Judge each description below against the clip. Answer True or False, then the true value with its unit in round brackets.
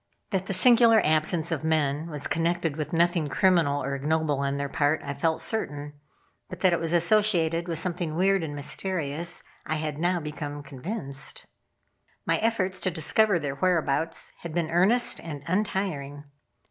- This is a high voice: False (165 Hz)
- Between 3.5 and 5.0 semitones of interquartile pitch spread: True (3.8 semitones)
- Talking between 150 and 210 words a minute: True (160 wpm)